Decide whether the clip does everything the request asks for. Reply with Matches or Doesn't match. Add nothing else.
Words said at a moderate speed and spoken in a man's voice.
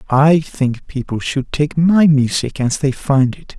Matches